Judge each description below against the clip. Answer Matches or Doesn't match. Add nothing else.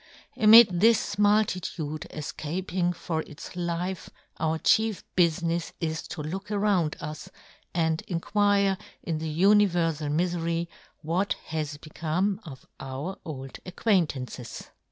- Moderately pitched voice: Matches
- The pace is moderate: Doesn't match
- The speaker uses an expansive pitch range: Doesn't match